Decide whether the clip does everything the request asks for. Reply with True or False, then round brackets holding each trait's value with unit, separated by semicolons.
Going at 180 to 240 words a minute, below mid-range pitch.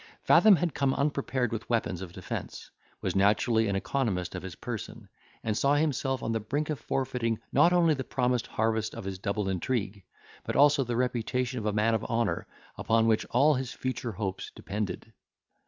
True (185 wpm; 115 Hz)